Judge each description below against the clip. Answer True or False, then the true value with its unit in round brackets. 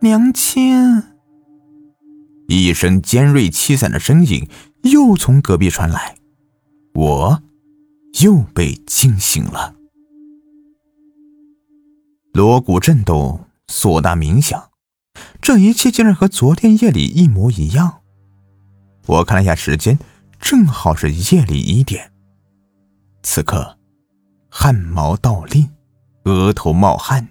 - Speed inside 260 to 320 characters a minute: False (150 characters per minute)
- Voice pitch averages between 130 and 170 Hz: True (140 Hz)